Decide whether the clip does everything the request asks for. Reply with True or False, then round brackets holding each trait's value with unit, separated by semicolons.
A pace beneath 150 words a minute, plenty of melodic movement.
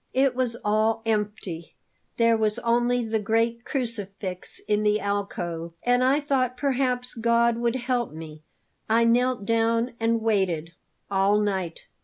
False (140 wpm; 3.1 semitones)